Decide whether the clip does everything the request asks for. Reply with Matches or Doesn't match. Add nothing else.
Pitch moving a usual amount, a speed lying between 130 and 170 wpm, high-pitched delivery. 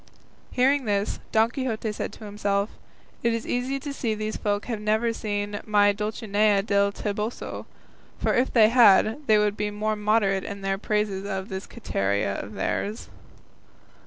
Doesn't match